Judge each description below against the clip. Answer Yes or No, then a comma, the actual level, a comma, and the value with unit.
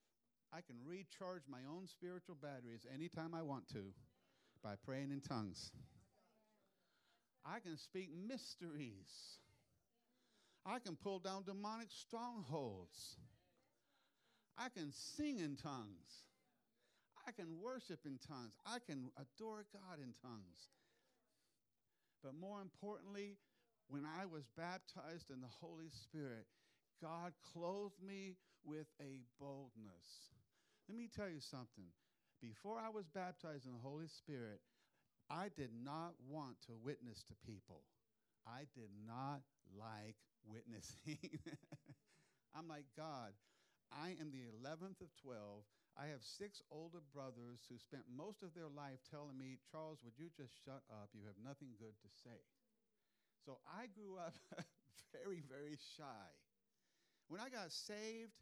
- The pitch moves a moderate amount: No, wide, 6.9 semitones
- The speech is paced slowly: Yes, slow, 130 wpm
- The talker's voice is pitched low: No, medium, 150 Hz